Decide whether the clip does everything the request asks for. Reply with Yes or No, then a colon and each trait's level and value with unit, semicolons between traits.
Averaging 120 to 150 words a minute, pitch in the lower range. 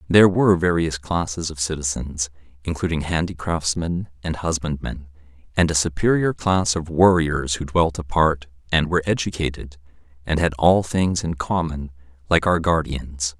Yes: average, 140 wpm; very low, 80 Hz